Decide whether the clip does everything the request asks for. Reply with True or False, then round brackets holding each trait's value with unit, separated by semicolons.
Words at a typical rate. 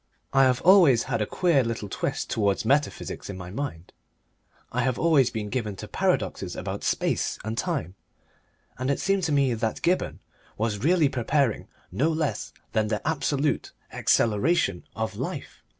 True (160 wpm)